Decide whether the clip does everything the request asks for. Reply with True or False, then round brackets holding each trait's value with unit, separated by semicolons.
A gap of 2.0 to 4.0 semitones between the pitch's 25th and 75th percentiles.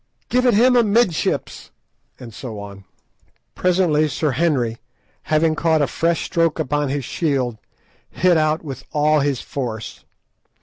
False (4.4 semitones)